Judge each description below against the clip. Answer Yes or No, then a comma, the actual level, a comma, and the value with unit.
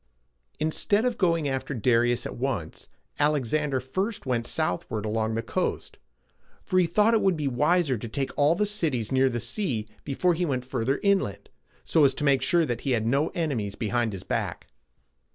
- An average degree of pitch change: No, wide, 5.9 semitones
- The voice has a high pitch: No, low, 135 Hz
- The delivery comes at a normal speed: Yes, average, 185 wpm